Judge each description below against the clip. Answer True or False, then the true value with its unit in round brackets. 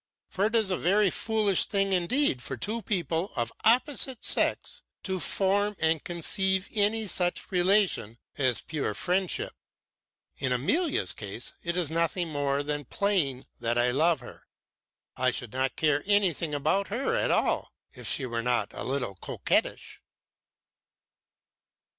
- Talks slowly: False (145 wpm)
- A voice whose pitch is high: False (175 Hz)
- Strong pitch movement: True (6.5 semitones)